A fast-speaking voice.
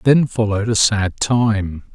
No: average, 155 wpm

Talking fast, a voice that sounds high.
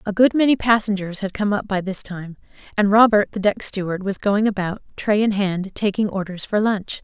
Yes: fast, 215 wpm; high, 200 Hz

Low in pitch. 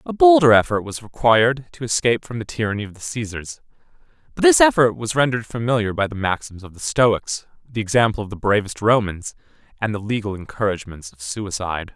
Yes: low, 110 Hz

